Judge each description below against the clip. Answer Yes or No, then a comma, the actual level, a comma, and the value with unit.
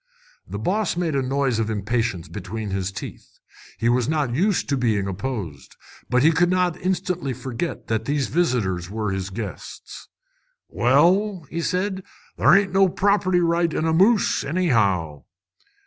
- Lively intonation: Yes, wide, 8.5 semitones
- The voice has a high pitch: No, low, 135 Hz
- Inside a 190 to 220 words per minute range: No, average, 155 wpm